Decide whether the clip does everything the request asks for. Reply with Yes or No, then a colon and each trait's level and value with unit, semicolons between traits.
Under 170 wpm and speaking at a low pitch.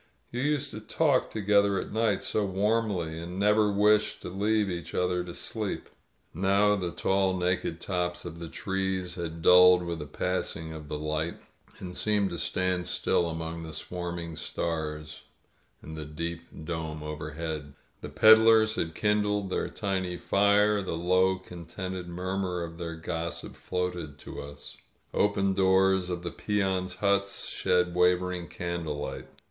Yes: average, 155 wpm; very low, 90 Hz